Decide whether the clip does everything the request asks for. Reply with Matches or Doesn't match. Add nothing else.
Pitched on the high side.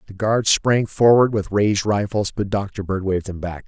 Doesn't match